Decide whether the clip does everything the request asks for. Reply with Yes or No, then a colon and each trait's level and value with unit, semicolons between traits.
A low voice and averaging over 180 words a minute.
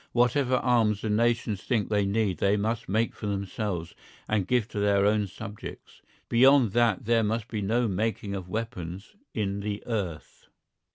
No: low, 105 Hz; average, 165 wpm